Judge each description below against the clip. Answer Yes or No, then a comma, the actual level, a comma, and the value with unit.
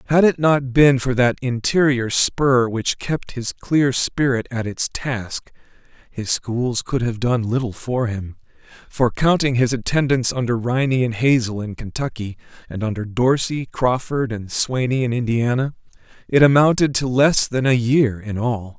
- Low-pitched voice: Yes, low, 125 Hz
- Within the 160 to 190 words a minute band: Yes, average, 165 wpm